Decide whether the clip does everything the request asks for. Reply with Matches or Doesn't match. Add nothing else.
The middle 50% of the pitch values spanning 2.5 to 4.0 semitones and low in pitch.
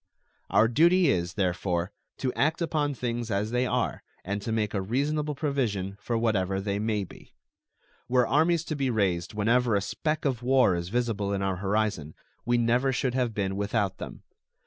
Doesn't match